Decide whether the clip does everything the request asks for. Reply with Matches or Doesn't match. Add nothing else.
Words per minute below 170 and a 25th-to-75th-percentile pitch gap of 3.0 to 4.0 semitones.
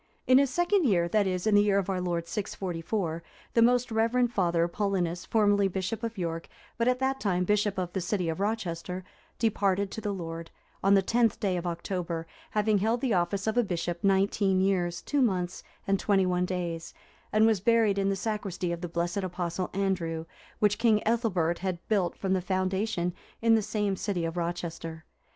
Doesn't match